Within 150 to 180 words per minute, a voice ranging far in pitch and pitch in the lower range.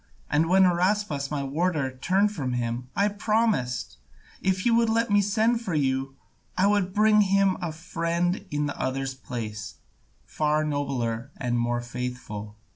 No: average, 155 wpm; wide, 7.4 semitones; medium, 155 Hz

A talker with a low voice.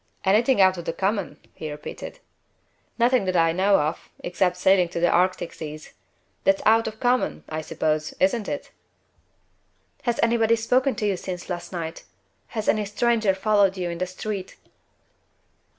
No: high, 190 Hz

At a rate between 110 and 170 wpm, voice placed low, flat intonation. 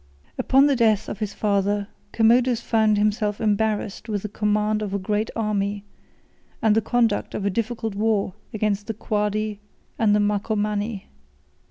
No: average, 155 wpm; high, 210 Hz; narrow, 1.3 semitones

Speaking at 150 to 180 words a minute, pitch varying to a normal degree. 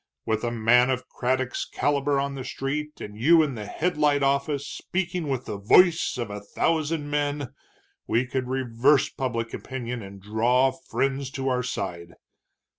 Yes: average, 160 wpm; average, 3.5 semitones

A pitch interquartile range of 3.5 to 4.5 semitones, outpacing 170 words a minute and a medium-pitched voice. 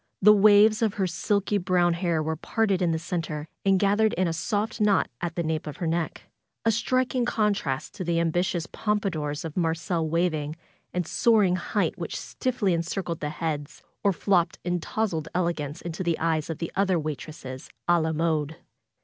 Yes: average, 3.8 semitones; average, 185 wpm; medium, 175 Hz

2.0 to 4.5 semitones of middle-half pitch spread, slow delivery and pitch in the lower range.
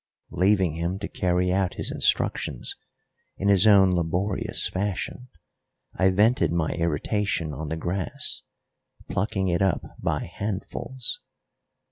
Yes: average, 2.7 semitones; slow, 120 wpm; very low, 95 Hz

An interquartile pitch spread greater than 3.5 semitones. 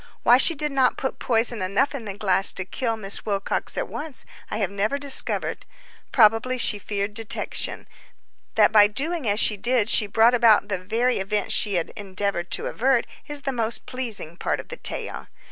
Yes: average, 4.0 semitones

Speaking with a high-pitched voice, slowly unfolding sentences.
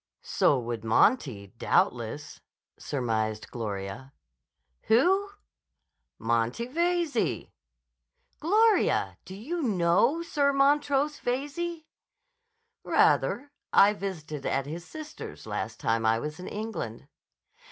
Yes: high, 195 Hz; slow, 95 wpm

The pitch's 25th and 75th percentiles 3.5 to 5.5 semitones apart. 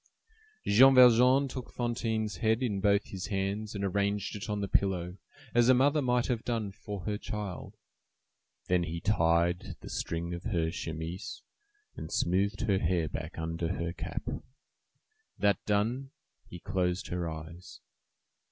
Yes: average, 4.4 semitones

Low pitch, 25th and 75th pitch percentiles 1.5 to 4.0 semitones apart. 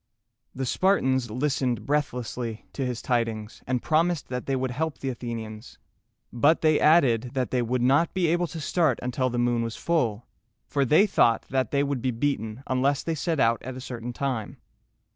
Yes: low, 130 Hz; average, 3.4 semitones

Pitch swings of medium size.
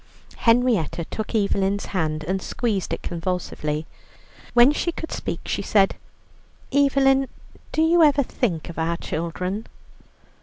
No: wide, 7.9 semitones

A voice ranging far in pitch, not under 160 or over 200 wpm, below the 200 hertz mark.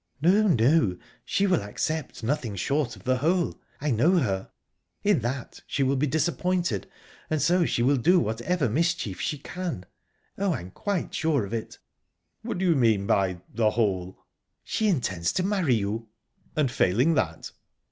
Yes: wide, 7.8 semitones; average, 165 wpm; low, 135 Hz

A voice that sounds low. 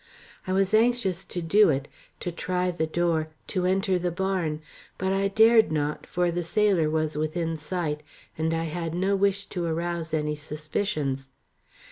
No: medium, 175 Hz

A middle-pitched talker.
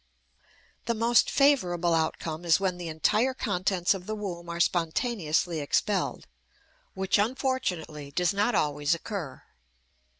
Yes: medium, 180 Hz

